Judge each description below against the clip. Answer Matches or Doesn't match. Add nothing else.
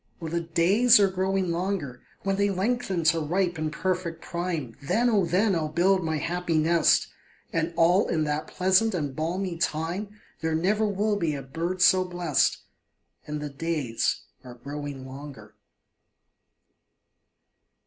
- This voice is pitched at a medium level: Matches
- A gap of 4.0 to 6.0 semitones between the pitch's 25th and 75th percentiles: Doesn't match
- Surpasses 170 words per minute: Doesn't match